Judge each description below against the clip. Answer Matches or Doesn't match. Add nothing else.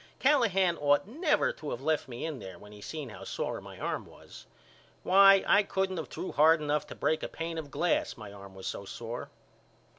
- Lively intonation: Matches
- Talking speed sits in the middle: Doesn't match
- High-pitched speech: Doesn't match